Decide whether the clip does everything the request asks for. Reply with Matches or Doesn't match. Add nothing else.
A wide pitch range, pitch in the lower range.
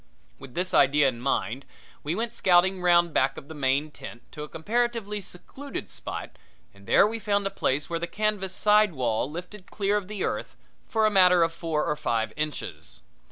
Doesn't match